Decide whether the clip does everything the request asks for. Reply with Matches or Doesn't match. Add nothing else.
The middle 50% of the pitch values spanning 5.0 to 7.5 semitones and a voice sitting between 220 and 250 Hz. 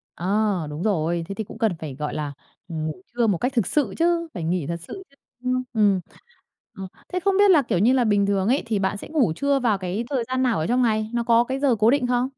Matches